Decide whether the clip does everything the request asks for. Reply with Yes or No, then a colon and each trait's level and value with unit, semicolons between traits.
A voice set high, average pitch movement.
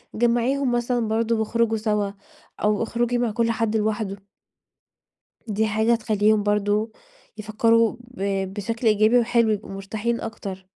No: high, 220 Hz; narrow, 1.8 semitones